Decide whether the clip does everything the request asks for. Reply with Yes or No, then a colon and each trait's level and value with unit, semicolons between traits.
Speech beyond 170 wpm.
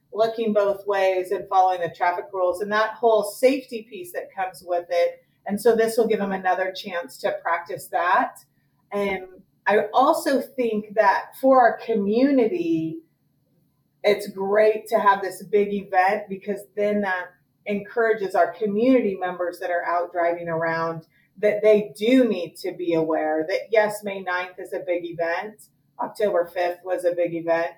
No: average, 165 wpm